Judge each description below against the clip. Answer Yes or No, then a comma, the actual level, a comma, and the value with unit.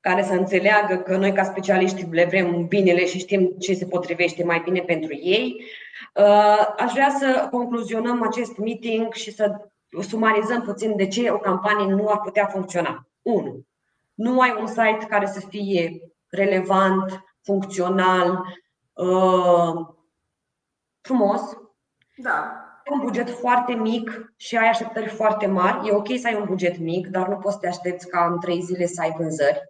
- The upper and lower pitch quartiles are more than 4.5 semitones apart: No, average, 3.3 semitones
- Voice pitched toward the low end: No, high, 195 Hz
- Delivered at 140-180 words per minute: Yes, average, 160 wpm